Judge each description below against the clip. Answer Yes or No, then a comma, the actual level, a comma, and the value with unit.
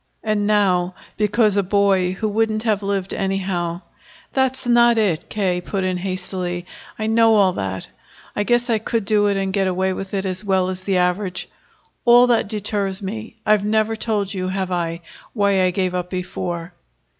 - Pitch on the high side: Yes, high, 195 Hz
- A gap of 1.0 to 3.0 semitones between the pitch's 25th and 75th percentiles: Yes, narrow, 2.6 semitones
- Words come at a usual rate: Yes, average, 185 wpm